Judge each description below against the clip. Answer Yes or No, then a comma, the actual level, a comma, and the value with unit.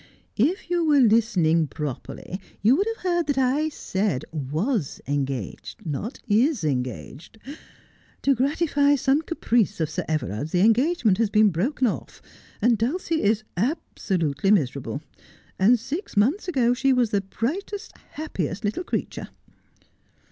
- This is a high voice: Yes, high, 225 Hz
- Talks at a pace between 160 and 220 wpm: No, average, 140 wpm